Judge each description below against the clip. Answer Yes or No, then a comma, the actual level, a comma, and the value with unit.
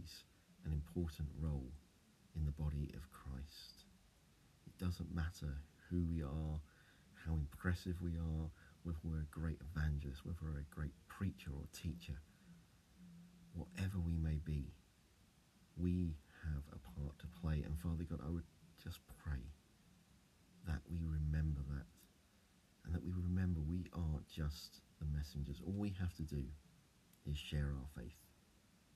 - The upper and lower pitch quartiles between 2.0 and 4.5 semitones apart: Yes, average, 2.9 semitones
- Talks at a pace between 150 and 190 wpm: No, average, 140 wpm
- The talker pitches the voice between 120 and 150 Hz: No, very low, 80 Hz